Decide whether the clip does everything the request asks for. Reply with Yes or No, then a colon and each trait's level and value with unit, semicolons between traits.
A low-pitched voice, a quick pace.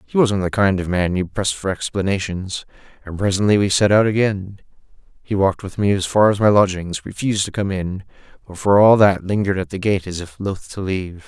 Yes: very low, 95 Hz; fast, 225 wpm